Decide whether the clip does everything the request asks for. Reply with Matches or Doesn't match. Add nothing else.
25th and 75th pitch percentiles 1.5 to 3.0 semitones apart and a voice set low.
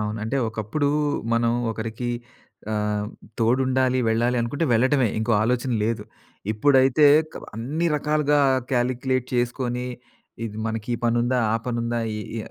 Matches